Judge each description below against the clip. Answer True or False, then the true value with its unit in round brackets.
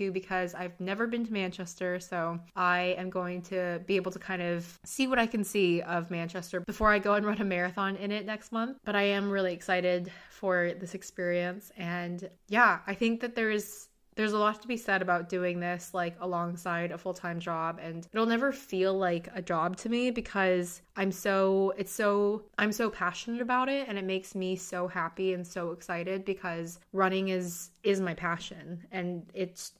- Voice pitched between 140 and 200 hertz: True (185 Hz)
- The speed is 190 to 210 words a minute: True (200 wpm)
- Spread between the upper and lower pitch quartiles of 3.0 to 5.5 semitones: False (2.4 semitones)